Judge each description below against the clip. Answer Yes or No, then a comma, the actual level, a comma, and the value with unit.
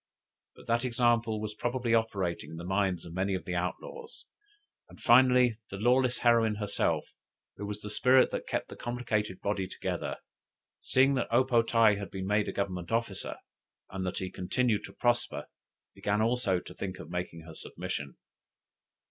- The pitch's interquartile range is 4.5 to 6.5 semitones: No, average, 4.1 semitones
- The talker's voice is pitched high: No, low, 105 Hz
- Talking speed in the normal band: Yes, average, 175 wpm